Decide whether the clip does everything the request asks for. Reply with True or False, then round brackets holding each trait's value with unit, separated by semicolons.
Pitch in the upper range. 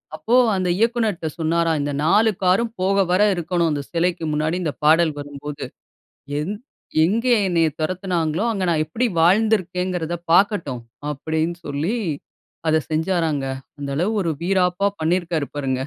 False (170 Hz)